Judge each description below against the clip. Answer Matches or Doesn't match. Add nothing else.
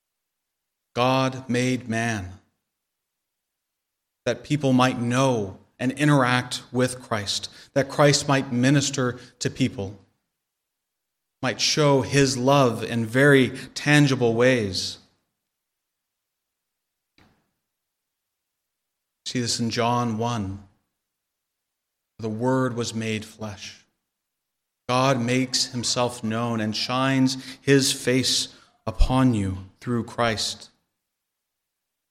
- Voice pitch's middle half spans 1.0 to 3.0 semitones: Matches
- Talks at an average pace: Doesn't match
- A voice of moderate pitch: Doesn't match